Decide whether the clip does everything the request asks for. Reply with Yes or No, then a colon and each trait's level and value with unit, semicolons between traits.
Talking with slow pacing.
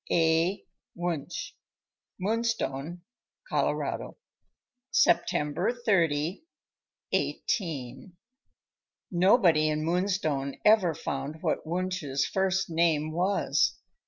Yes: slow, 75 wpm